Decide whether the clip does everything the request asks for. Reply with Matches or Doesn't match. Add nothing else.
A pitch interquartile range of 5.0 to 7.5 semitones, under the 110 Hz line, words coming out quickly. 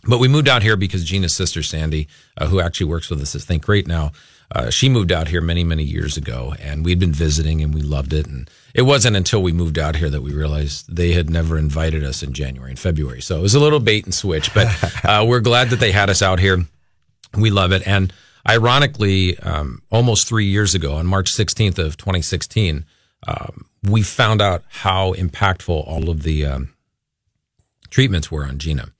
Matches